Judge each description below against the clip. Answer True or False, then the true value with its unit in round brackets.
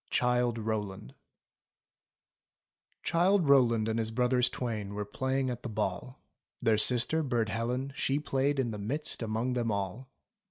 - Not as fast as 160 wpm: True (145 wpm)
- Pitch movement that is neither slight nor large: True (3.2 semitones)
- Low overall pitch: True (120 Hz)